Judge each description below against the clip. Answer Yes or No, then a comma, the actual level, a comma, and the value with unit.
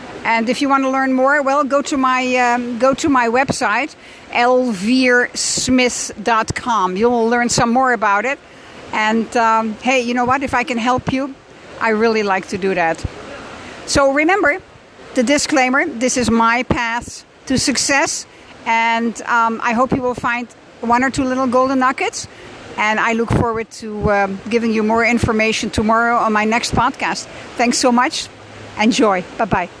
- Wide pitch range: No, narrow, 2.4 semitones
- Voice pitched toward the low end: No, high, 245 Hz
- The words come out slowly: No, average, 165 wpm